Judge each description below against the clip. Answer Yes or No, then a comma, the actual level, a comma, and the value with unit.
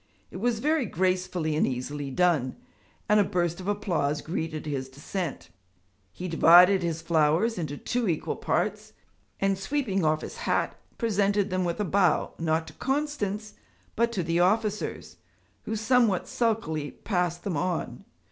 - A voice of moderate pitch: Yes, medium, 180 Hz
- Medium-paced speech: Yes, average, 150 wpm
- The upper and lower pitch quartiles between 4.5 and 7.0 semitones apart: Yes, average, 4.8 semitones